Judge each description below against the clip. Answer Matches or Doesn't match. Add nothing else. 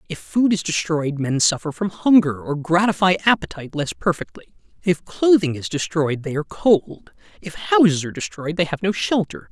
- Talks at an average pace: Matches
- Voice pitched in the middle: Matches